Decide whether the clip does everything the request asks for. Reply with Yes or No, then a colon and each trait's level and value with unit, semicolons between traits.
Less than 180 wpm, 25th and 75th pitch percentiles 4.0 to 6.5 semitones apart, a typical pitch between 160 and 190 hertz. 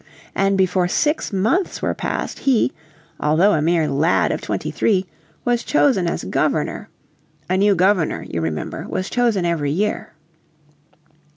Yes: average, 145 wpm; average, 4.3 semitones; medium, 185 Hz